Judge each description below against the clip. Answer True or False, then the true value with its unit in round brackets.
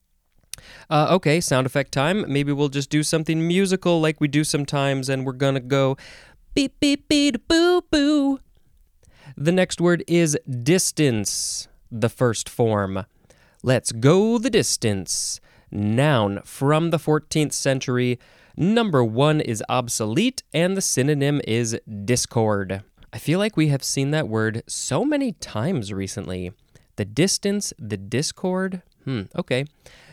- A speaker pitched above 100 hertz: True (140 Hz)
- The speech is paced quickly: False (135 wpm)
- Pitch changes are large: True (6.5 semitones)